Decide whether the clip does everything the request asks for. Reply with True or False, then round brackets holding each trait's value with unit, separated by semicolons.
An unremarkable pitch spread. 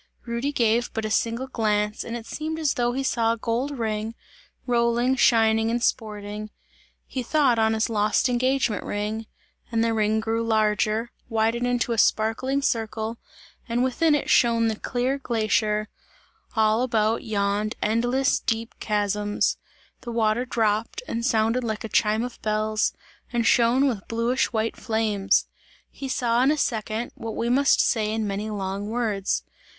False (2.1 semitones)